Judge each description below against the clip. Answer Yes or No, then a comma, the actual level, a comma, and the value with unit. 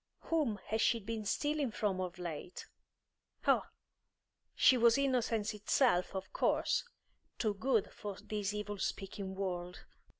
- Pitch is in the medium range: No, high, 210 Hz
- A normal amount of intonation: Yes, average, 3.5 semitones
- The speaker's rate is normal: No, slow, 130 wpm